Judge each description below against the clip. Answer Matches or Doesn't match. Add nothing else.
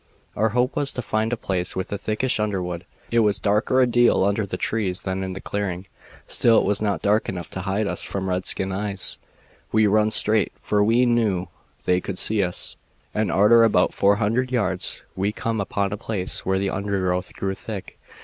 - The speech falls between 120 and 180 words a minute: Doesn't match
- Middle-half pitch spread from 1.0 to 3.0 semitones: Matches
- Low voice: Matches